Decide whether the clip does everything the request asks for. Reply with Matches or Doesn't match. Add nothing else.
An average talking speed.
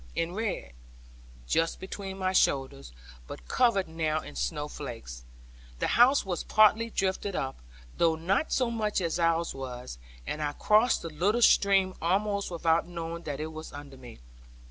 Matches